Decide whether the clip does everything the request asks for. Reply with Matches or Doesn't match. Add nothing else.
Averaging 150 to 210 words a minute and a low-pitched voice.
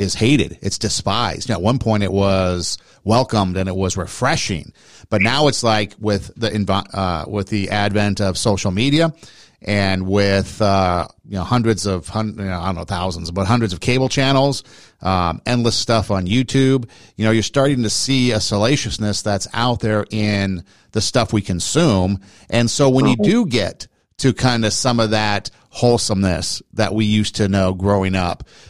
Matches